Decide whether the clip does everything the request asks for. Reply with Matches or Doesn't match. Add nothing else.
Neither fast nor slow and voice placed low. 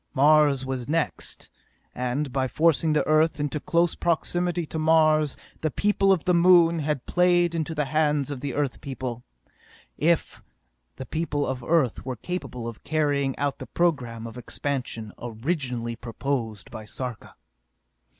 Doesn't match